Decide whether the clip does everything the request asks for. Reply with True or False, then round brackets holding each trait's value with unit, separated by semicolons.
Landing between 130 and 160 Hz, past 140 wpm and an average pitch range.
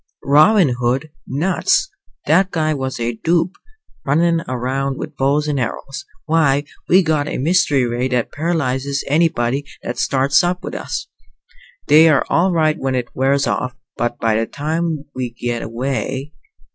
True (140 Hz; 150 wpm; 3.8 semitones)